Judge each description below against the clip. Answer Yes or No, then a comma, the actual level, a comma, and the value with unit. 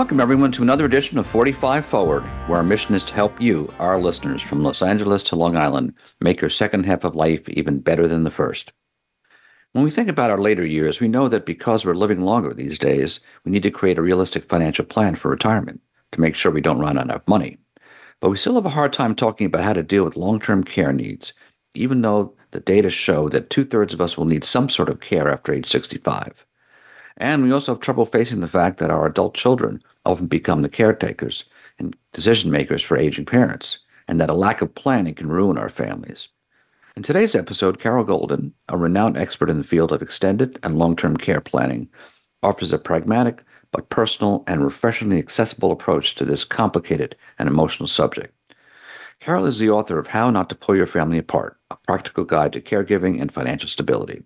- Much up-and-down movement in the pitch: Yes, wide, 5.9 semitones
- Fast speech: Yes, fast, 210 wpm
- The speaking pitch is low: Yes, low, 100 Hz